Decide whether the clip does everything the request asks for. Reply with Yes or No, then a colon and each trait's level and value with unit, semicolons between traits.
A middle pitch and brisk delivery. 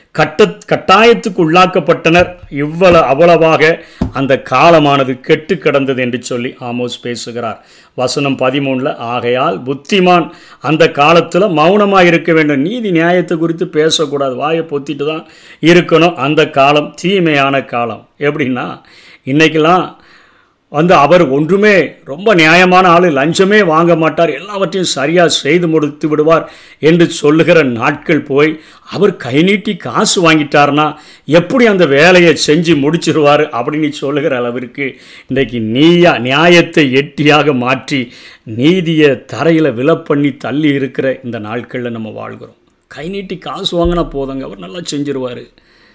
No: medium, 155 Hz; average, 115 wpm